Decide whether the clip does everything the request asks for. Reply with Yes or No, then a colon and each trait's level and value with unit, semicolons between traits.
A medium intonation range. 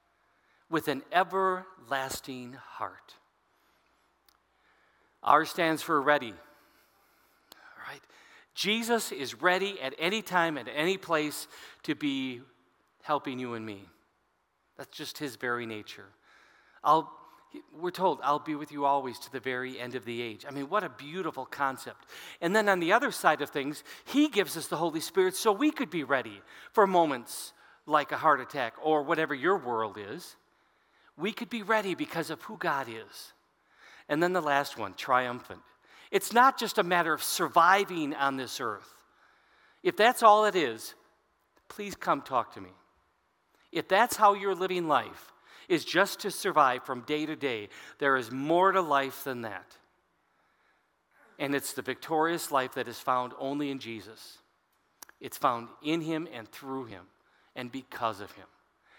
No: wide, 6.1 semitones